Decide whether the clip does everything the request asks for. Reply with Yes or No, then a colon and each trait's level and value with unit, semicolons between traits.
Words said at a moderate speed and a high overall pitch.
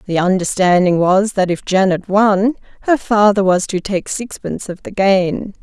Yes: average, 170 wpm; high, 195 Hz